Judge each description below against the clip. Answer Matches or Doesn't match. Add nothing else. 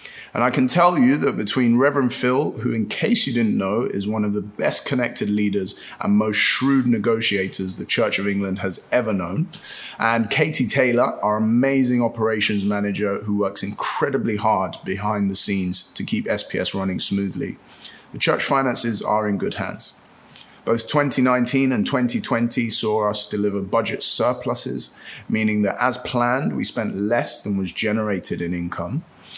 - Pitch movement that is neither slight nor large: Matches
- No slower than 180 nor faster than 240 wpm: Doesn't match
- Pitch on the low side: Matches